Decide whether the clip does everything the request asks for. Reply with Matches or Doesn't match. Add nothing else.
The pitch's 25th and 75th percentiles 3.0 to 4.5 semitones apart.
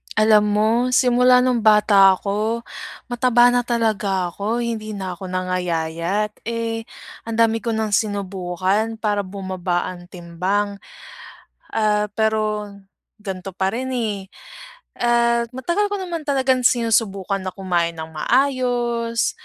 Matches